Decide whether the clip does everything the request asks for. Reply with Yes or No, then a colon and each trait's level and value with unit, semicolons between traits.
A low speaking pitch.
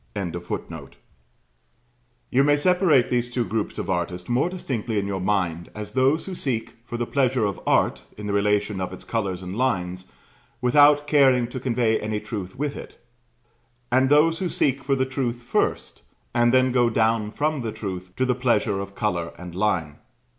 Yes: low, 115 Hz